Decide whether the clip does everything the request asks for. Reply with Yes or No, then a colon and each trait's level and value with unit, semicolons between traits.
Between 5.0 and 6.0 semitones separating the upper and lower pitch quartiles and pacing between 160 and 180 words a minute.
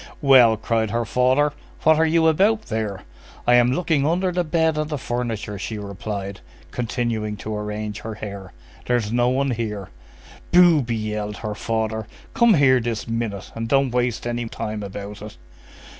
No: average, 4.5 semitones; average, 165 wpm